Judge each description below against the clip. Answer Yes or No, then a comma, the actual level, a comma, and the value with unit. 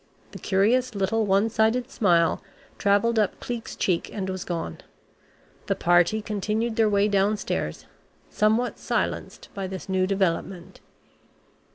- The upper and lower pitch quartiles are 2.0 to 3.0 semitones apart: Yes, average, 2.7 semitones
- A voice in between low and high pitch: No, high, 200 Hz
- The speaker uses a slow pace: Yes, slow, 130 wpm